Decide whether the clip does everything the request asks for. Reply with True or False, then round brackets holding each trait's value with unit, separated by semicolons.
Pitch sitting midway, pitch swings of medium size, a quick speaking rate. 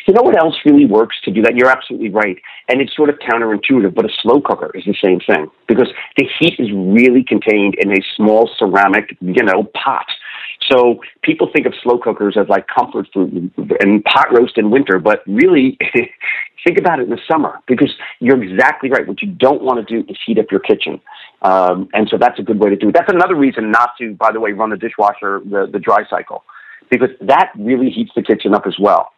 False (115 Hz; 3.6 semitones; 225 wpm)